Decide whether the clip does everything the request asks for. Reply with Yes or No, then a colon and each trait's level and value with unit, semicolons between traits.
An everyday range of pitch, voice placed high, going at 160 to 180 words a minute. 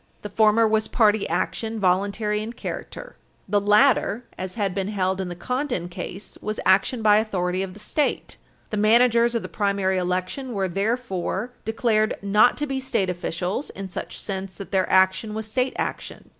Yes: average, 3.1 semitones; high, 210 Hz; average, 175 wpm